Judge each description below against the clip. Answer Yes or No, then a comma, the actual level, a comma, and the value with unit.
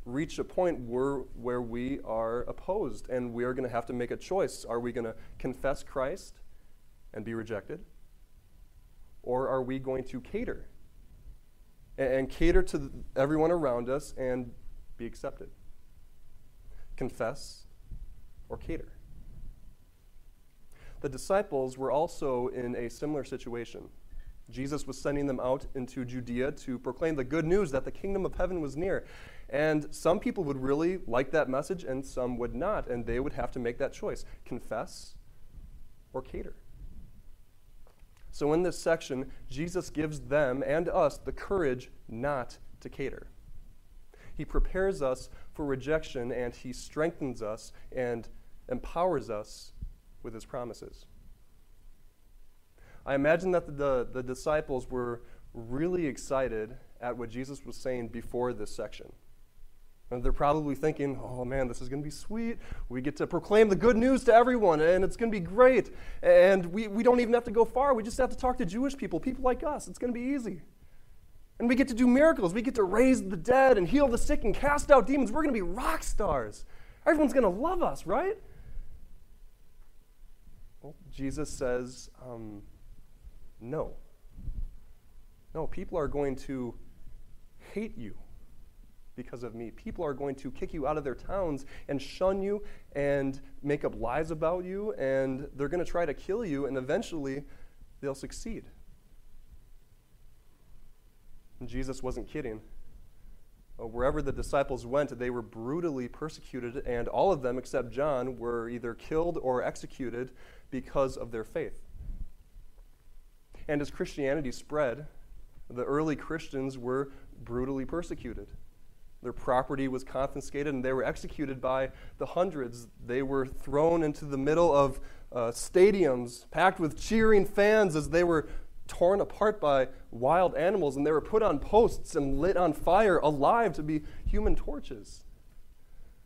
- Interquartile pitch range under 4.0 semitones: No, wide, 5.5 semitones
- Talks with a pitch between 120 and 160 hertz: Yes, low, 135 Hz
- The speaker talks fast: No, average, 155 wpm